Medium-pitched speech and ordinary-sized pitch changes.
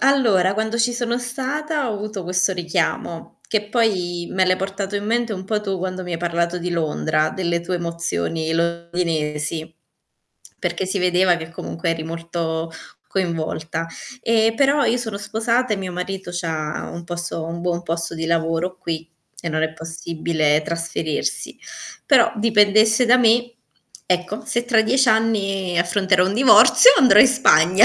Yes: medium, 180 Hz; average, 4.7 semitones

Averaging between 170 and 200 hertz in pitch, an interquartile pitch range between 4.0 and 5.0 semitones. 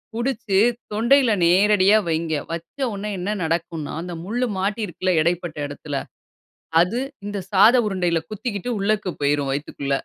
Yes: high, 190 Hz; average, 4.3 semitones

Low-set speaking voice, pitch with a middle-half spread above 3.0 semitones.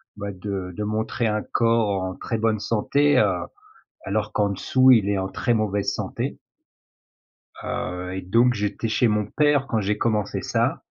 No: low, 105 Hz; average, 2.7 semitones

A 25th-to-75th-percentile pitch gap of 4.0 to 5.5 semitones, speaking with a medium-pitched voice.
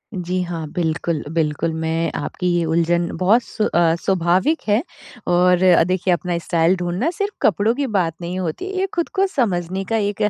No: average, 3.2 semitones; medium, 180 Hz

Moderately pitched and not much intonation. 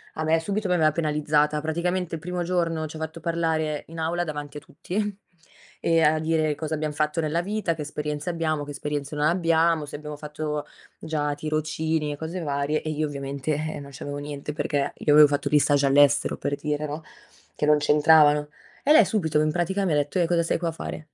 Yes: medium, 155 Hz; narrow, 1.9 semitones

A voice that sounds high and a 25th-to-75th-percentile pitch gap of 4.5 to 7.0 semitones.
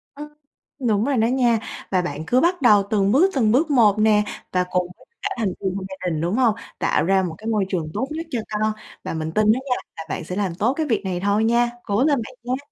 Yes: high, 215 Hz; average, 4.9 semitones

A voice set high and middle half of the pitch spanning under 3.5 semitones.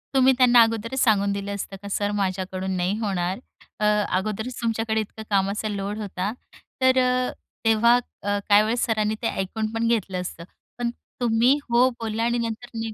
Yes: high, 220 Hz; average, 2.7 semitones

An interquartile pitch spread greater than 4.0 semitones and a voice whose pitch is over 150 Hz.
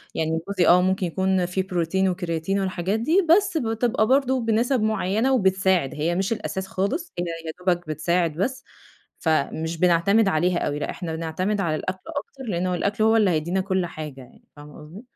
Yes: average, 4.4 semitones; medium, 185 Hz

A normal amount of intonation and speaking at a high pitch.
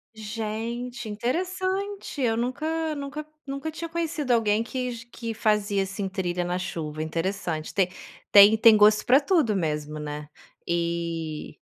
No: wide, 7.2 semitones; high, 220 Hz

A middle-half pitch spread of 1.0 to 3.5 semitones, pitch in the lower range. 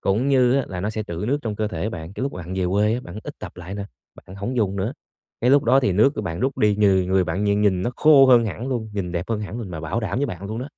No: average, 4.4 semitones; low, 105 Hz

